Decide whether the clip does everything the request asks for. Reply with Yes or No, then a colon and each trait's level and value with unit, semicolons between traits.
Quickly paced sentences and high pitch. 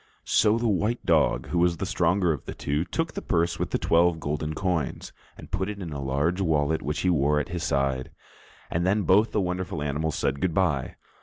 No: fast, 220 wpm; very low, 85 Hz